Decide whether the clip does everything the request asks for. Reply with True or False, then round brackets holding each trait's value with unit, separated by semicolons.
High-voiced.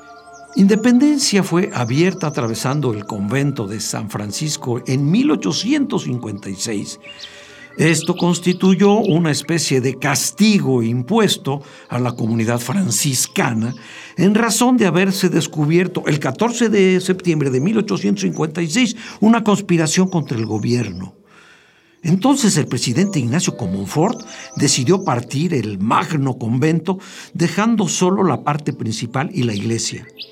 False (160 Hz)